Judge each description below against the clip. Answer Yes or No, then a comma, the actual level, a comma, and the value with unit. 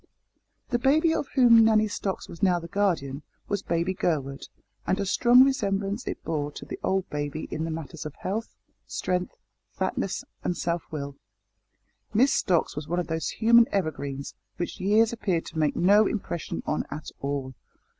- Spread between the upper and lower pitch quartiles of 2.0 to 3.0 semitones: No, wide, 5.5 semitones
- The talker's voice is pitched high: No, medium, 180 Hz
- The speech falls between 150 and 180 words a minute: Yes, average, 170 wpm